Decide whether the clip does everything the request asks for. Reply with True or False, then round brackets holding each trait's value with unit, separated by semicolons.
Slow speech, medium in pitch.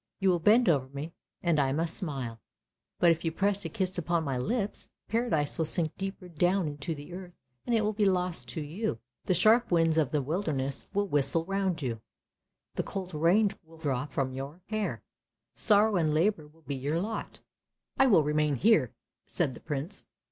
False (200 wpm; 165 Hz)